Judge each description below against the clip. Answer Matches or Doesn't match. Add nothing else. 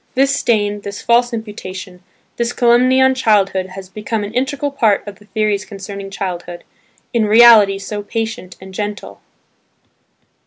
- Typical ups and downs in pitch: Matches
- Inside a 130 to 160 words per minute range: Matches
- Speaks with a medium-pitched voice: Doesn't match